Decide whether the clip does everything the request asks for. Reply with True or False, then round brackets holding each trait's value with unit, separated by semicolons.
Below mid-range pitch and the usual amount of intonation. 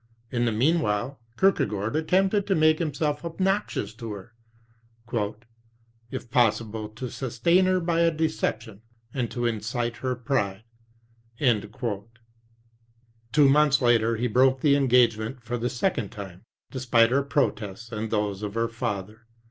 True (120 Hz; 4.3 semitones)